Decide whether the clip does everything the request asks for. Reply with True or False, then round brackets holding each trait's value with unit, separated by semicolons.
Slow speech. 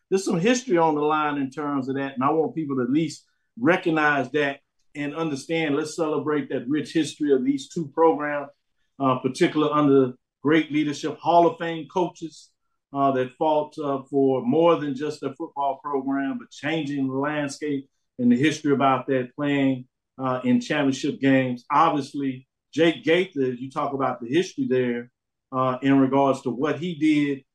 False (175 wpm)